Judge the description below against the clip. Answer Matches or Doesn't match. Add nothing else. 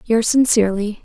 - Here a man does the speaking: Doesn't match